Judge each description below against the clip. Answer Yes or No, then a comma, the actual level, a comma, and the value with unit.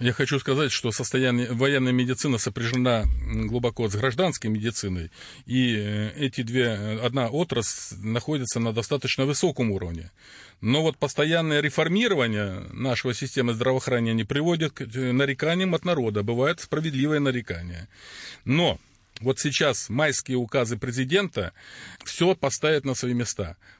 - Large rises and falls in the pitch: No, average, 3.9 semitones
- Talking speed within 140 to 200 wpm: No, average, 120 wpm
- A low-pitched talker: Yes, low, 125 Hz